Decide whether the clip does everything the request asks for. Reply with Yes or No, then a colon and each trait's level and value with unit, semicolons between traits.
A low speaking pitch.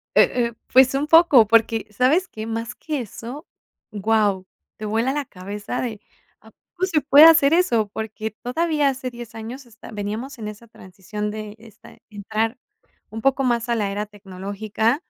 No: high, 225 Hz